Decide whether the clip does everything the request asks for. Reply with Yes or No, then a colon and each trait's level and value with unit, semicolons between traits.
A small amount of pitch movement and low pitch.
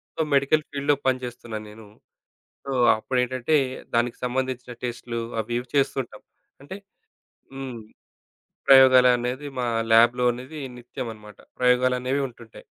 Yes: narrow, 1.9 semitones; low, 125 Hz